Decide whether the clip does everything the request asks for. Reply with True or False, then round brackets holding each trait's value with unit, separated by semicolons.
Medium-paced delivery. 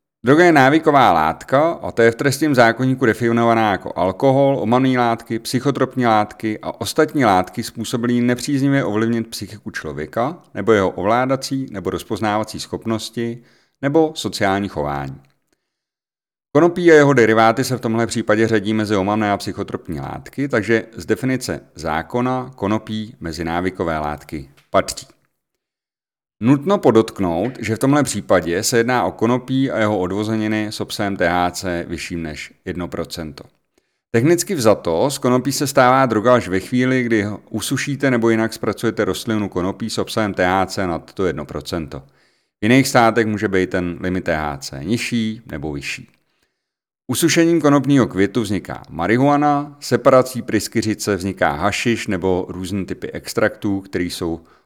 True (135 wpm)